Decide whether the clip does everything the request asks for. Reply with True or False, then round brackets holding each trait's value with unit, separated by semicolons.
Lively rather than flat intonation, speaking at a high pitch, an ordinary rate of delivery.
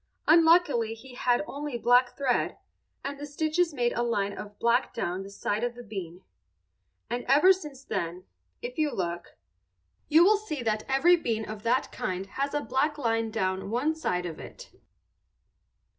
True (5.9 semitones; 245 Hz; 170 wpm)